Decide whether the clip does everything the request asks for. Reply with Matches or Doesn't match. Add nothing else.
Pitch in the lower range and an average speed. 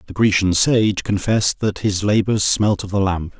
Matches